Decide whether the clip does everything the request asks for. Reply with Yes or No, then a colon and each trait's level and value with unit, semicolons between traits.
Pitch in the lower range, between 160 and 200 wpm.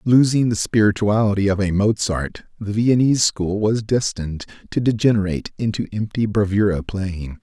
No: low, 105 Hz; slow, 135 wpm